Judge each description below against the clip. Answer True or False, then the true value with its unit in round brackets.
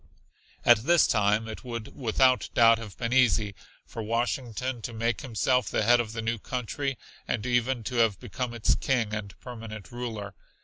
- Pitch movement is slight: True (2.2 semitones)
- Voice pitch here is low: True (115 Hz)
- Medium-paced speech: True (175 wpm)